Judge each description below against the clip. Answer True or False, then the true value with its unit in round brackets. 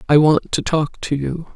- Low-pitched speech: False (150 Hz)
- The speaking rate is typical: False (230 wpm)